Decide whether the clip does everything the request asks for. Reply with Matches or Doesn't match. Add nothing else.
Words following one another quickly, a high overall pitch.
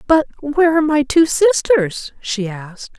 Doesn't match